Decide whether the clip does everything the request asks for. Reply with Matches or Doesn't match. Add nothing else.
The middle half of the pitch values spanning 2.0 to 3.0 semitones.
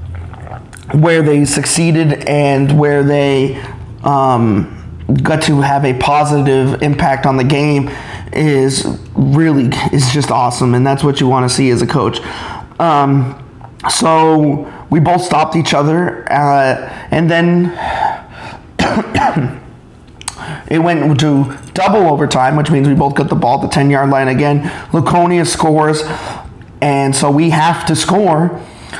Matches